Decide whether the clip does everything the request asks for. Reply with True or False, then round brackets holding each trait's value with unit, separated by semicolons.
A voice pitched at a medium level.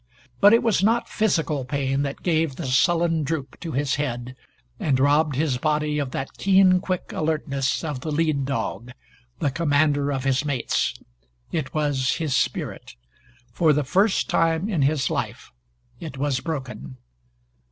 True (145 Hz)